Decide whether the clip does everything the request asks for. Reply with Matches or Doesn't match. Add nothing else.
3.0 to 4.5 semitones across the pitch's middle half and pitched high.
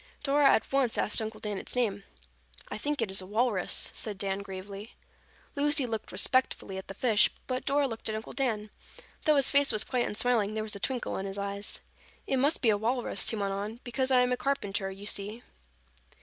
Matches